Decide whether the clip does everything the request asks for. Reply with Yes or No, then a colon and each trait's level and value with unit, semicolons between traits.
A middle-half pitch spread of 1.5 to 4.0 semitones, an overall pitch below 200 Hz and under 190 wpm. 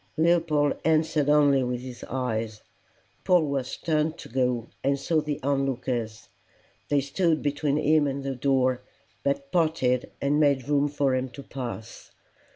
Yes: average, 2.9 semitones; medium, 140 Hz; average, 150 wpm